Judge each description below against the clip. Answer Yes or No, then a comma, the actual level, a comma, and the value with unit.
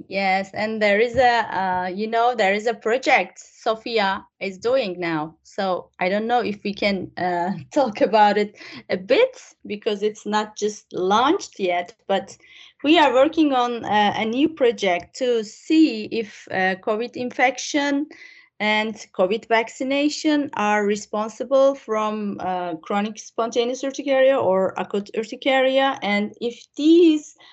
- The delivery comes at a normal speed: Yes, average, 145 wpm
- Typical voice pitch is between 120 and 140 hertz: No, high, 220 Hz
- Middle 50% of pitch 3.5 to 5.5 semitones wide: Yes, average, 4.7 semitones